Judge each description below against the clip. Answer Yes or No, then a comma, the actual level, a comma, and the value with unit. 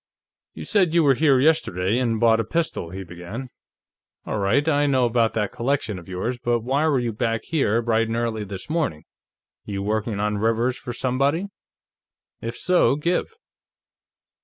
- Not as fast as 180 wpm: Yes, average, 170 wpm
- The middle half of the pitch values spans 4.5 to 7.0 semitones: Yes, average, 4.8 semitones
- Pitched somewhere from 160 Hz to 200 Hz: No, low, 120 Hz